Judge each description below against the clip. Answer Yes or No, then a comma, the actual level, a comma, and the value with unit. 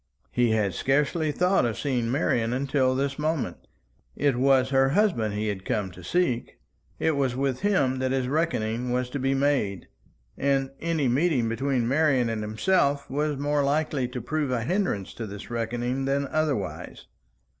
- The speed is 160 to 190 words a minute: Yes, average, 165 wpm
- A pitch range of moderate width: Yes, average, 3.4 semitones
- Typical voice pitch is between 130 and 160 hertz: Yes, low, 135 Hz